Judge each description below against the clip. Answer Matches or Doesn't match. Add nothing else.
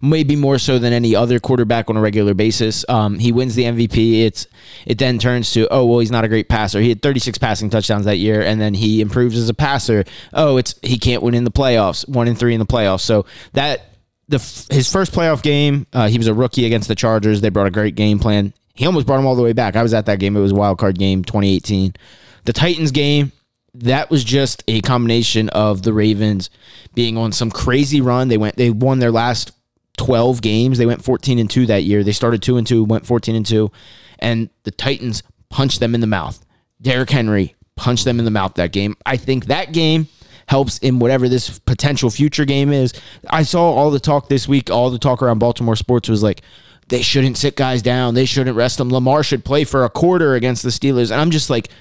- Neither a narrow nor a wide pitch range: Matches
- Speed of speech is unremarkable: Doesn't match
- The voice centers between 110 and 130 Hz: Matches